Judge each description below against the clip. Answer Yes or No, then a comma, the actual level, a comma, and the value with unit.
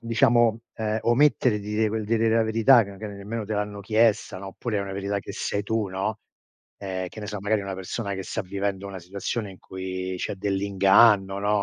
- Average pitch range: No, narrow, 2.2 semitones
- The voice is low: Yes, low, 105 Hz